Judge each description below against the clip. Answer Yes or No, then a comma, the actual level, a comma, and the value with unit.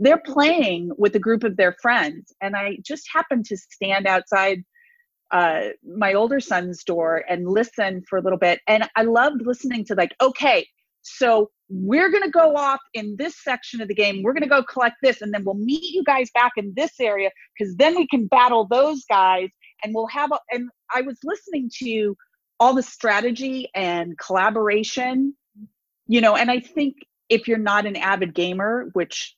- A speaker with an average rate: Yes, average, 190 wpm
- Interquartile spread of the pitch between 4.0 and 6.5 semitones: Yes, wide, 5.4 semitones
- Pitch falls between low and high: No, high, 230 Hz